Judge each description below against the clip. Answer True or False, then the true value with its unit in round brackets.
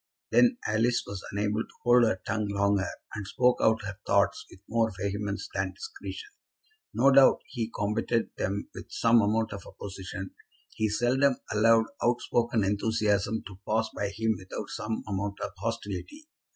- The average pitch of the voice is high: False (110 Hz)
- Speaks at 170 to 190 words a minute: False (160 wpm)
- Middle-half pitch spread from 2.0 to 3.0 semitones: True (2.6 semitones)